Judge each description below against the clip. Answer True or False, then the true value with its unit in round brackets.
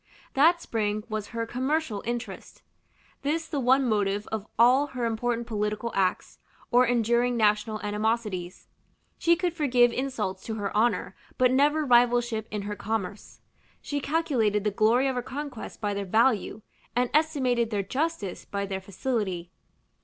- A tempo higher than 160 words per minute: False (150 wpm)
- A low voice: False (235 Hz)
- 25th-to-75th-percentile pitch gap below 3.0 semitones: False (3.9 semitones)